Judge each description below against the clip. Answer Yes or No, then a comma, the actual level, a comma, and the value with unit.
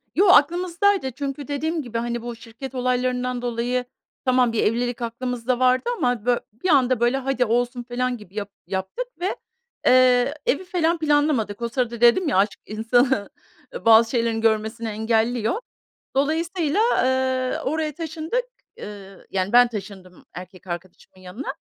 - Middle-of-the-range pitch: No, high, 245 Hz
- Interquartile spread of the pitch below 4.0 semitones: Yes, average, 3.6 semitones